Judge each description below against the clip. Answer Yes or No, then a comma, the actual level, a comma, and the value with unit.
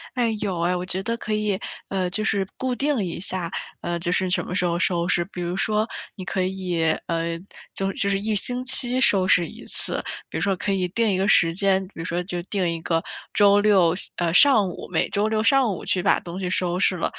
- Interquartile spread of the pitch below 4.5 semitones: Yes, average, 3.0 semitones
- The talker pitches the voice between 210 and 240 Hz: No, high, 190 Hz